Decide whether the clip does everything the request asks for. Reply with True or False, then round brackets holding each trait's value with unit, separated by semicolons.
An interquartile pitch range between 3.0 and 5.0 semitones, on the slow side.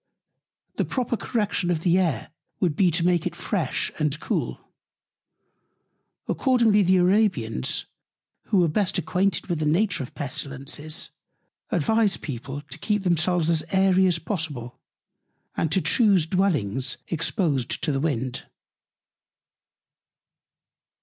True (4.6 semitones; 125 wpm)